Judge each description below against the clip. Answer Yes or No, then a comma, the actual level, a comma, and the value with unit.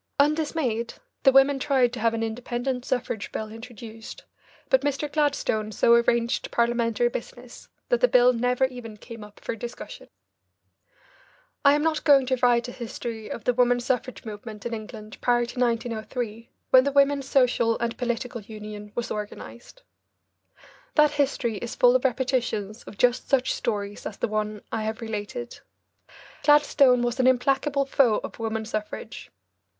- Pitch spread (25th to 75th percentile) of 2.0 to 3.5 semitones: Yes, average, 2.8 semitones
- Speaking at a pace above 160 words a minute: No, average, 155 wpm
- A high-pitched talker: Yes, high, 240 Hz